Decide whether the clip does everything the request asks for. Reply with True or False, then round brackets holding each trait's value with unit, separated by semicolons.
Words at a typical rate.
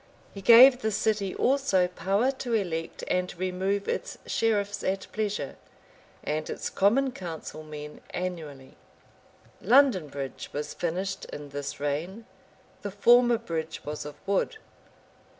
False (130 wpm)